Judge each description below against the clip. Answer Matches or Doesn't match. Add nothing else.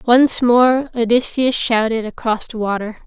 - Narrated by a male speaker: Doesn't match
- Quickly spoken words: Doesn't match